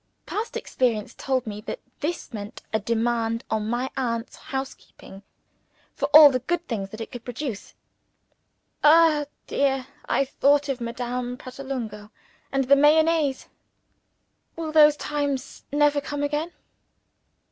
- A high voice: Yes, very high, 265 Hz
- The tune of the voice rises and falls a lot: No, average, 4.0 semitones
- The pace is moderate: No, slow, 130 wpm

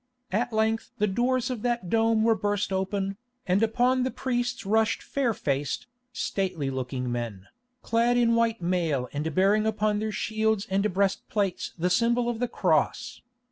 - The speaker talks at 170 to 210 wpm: No, average, 160 wpm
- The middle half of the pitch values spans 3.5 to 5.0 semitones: Yes, average, 4.0 semitones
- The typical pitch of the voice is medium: No, high, 210 Hz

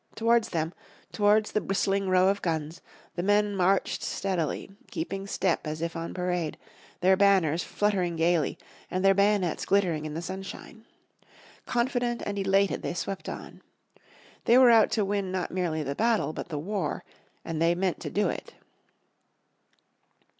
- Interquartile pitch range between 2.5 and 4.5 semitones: Yes, average, 3.4 semitones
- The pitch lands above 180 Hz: Yes, high, 190 Hz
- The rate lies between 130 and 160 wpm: Yes, average, 155 wpm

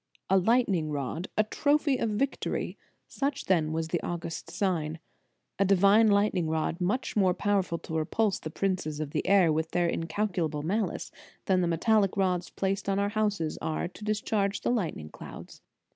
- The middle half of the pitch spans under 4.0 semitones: No, average, 4.3 semitones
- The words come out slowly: No, average, 175 wpm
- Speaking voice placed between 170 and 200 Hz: Yes, high, 190 Hz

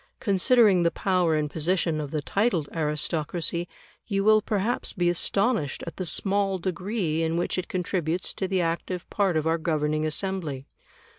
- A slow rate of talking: No, average, 160 wpm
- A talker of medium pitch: Yes, medium, 175 Hz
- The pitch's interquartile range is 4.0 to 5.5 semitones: No, average, 3.5 semitones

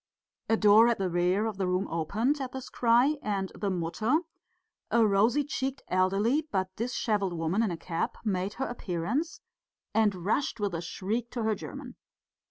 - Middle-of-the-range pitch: No, high, 210 Hz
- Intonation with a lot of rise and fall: No, average, 4.6 semitones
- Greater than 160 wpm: Yes, average, 180 wpm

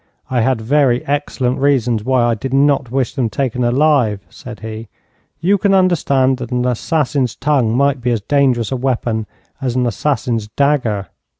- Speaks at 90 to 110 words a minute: No, average, 170 wpm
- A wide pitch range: No, average, 3.1 semitones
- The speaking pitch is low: Yes, low, 125 Hz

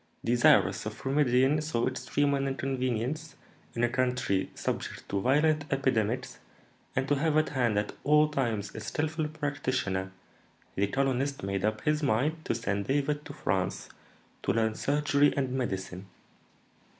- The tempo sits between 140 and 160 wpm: Yes, average, 145 wpm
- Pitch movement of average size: Yes, average, 4.7 semitones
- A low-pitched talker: Yes, low, 130 Hz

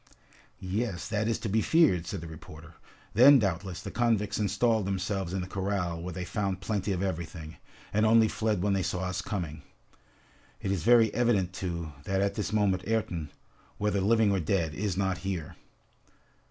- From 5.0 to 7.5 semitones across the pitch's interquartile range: No, average, 3.1 semitones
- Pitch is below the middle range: Yes, very low, 95 Hz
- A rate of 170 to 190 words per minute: Yes, average, 180 wpm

